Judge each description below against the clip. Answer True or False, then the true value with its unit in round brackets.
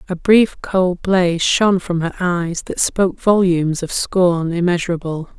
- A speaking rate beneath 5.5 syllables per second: True (4.5 syllables/s)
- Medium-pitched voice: True (180 Hz)